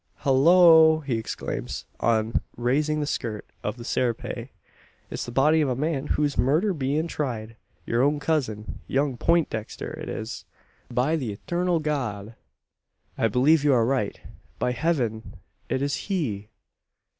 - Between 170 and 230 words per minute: No, average, 145 wpm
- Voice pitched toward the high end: No, low, 135 Hz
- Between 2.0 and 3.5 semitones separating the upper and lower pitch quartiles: No, average, 5.1 semitones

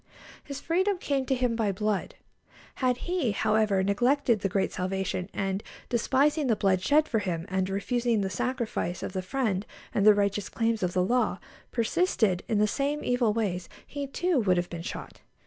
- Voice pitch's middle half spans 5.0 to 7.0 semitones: Yes, average, 5.3 semitones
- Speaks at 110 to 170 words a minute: No, average, 180 wpm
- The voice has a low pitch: No, high, 215 Hz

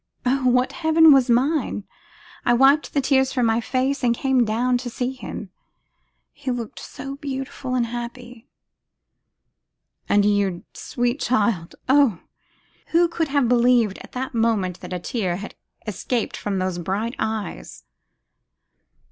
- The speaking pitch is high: Yes, high, 245 Hz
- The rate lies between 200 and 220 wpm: No, average, 140 wpm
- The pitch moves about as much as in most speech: Yes, average, 3.6 semitones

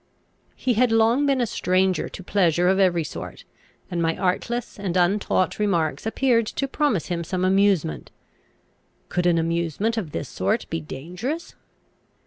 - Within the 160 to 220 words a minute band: No, average, 150 wpm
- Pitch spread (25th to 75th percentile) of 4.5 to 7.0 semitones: Yes, average, 4.8 semitones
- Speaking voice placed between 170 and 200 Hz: Yes, medium, 185 Hz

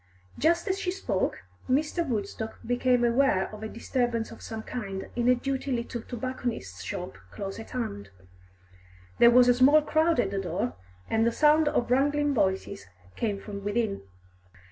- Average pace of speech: Yes, average, 165 wpm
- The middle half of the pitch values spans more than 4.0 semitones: Yes, average, 4.8 semitones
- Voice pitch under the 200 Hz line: No, high, 240 Hz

